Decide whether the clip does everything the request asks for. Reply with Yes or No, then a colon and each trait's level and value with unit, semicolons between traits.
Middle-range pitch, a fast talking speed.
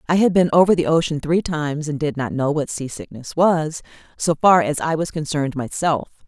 Yes: medium, 155 Hz; fast, 210 wpm